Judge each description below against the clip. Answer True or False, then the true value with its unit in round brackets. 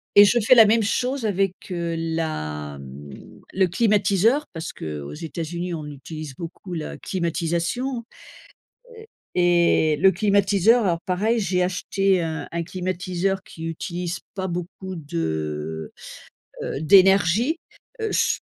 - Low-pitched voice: False (180 Hz)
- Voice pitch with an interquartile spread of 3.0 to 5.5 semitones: True (3.7 semitones)